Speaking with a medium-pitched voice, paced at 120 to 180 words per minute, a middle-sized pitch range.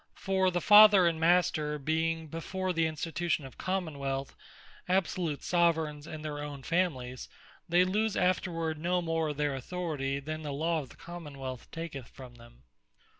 Yes: medium, 160 Hz; average, 165 wpm; average, 3.4 semitones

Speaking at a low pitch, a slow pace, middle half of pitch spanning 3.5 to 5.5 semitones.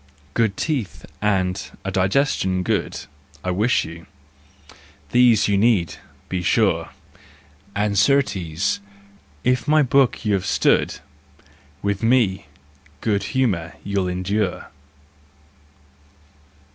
Yes: low, 100 Hz; slow, 95 wpm; average, 4.3 semitones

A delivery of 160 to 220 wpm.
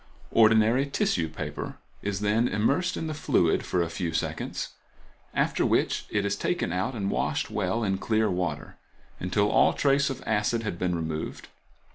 Yes: average, 165 wpm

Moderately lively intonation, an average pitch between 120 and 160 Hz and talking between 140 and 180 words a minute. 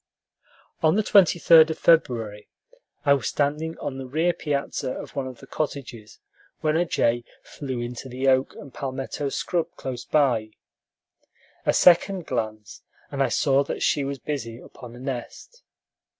Yes: average, 4.2 semitones; medium, 140 Hz; average, 155 wpm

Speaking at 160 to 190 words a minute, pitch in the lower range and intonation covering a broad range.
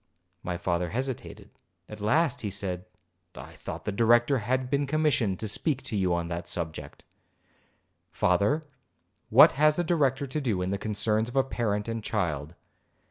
Yes: average, 165 wpm; low, 110 Hz; wide, 6.3 semitones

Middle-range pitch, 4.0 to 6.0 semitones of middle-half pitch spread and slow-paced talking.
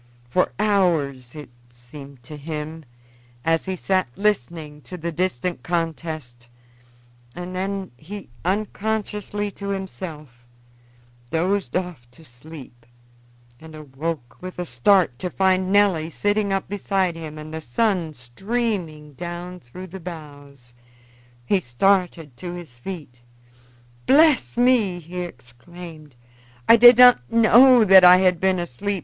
Yes: medium, 175 Hz; average, 4.6 semitones; slow, 130 wpm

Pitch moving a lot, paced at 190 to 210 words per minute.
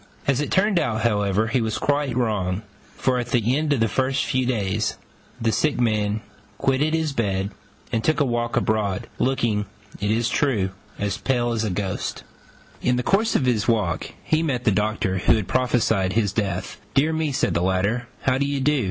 No: average, 4.4 semitones; average, 195 wpm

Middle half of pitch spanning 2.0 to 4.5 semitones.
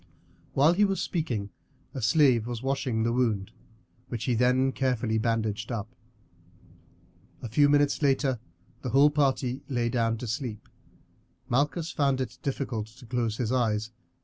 Yes: average, 3.3 semitones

